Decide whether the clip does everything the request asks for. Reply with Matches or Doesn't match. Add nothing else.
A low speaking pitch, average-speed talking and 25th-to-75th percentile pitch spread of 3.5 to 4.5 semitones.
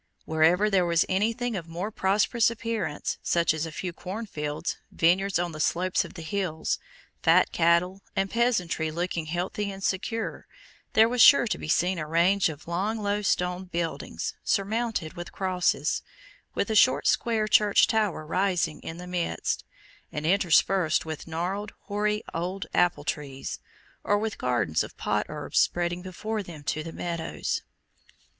Doesn't match